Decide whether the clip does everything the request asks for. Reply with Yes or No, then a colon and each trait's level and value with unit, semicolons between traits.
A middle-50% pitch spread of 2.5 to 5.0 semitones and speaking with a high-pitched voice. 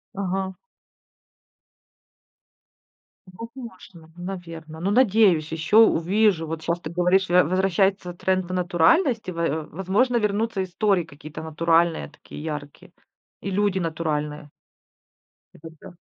No: average, 3.3 semitones; medium, 180 Hz